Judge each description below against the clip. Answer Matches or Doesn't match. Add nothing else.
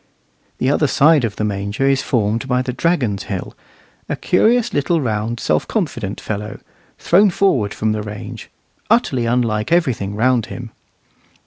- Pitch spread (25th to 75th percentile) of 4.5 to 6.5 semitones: Matches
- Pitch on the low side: Matches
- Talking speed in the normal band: Matches